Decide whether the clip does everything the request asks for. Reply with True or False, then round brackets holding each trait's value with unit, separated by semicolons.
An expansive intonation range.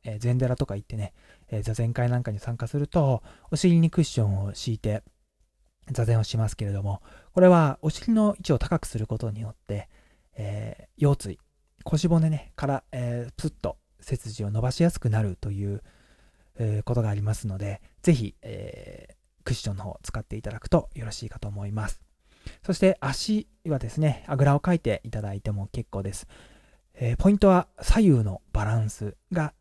True (5.9 semitones)